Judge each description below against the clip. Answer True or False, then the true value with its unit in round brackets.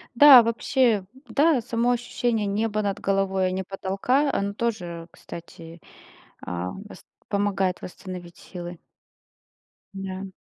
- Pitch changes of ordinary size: True (3.9 semitones)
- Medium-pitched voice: False (195 Hz)